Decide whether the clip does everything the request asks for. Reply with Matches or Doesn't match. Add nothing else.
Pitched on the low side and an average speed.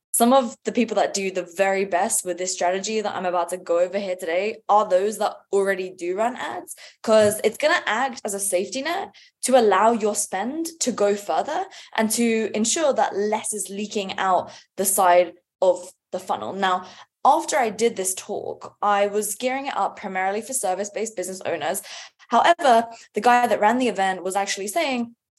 Doesn't match